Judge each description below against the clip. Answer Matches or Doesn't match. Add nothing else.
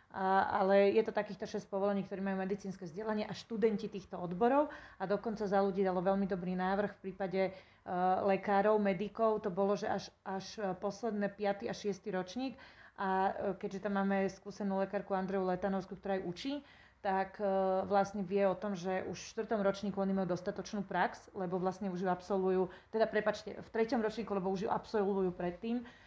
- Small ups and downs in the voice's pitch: Matches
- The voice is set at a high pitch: Matches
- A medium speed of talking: Doesn't match